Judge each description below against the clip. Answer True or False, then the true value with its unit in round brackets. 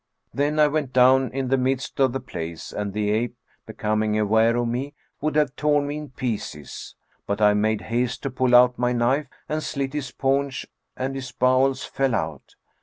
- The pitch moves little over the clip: False (3.5 semitones)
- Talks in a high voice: False (130 Hz)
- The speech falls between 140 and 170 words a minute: False (190 wpm)